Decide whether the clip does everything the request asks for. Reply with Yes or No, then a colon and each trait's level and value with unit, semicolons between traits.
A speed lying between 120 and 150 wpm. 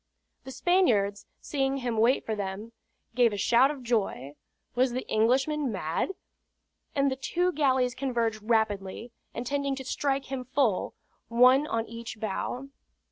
Yes: average, 140 wpm